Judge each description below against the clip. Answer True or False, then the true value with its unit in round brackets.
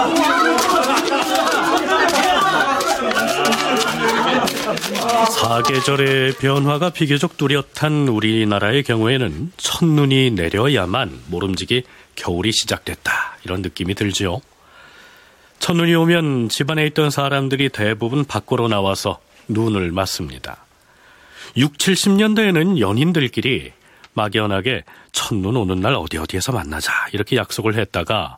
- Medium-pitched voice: False (125 Hz)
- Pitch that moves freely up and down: True (6.2 semitones)